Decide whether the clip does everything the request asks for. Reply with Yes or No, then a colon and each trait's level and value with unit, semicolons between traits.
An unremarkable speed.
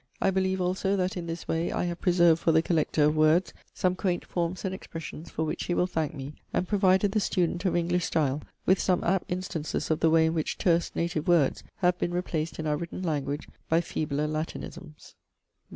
No: fast, 210 wpm